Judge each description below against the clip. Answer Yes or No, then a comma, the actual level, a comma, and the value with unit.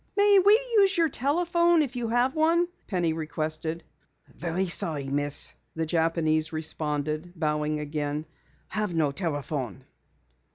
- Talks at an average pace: No, slow, 130 wpm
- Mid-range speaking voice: Yes, medium, 165 Hz